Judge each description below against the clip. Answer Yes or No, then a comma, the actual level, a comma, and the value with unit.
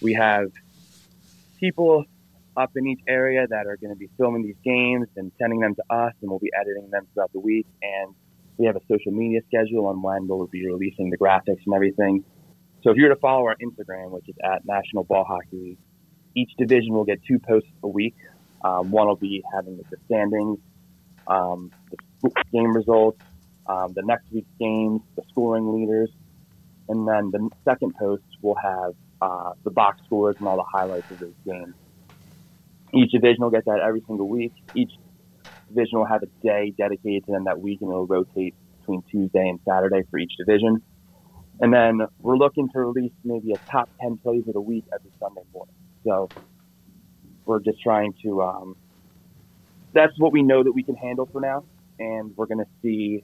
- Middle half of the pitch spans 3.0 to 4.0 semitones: Yes, average, 3.5 semitones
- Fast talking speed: No, average, 190 wpm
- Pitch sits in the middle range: No, low, 105 Hz